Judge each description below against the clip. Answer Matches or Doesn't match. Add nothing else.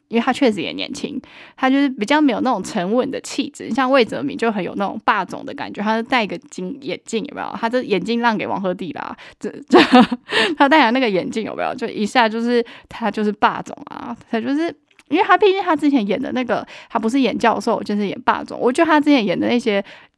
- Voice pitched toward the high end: Matches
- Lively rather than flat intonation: Doesn't match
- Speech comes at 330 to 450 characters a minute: Matches